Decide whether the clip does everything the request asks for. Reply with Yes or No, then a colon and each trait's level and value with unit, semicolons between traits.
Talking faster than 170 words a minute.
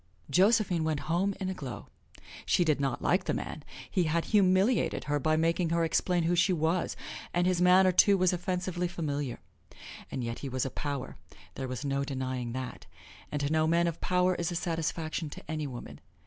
Yes: average, 195 wpm